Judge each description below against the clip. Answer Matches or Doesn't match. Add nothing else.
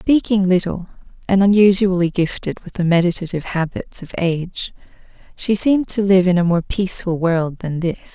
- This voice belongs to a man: Doesn't match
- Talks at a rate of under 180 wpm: Matches